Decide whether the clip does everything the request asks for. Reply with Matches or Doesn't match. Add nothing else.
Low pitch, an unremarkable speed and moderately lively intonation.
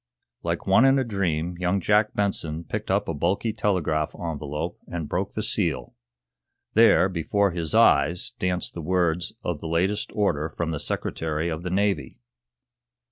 Matches